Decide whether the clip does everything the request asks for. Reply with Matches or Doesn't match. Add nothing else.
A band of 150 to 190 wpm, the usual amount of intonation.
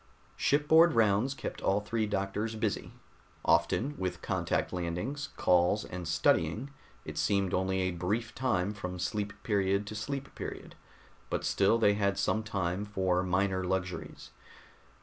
Doesn't match